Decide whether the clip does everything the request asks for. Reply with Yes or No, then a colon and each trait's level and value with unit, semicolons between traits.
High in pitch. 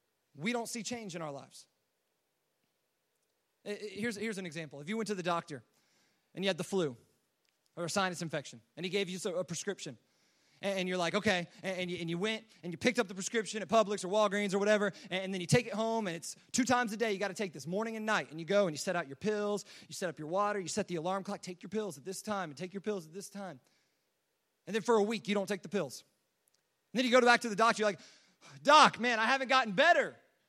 Yes: high, 200 Hz